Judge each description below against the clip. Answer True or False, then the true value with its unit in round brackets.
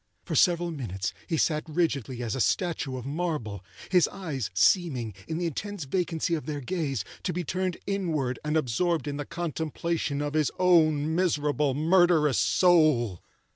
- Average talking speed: True (160 wpm)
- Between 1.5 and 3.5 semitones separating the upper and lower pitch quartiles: False (4.1 semitones)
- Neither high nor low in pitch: True (155 Hz)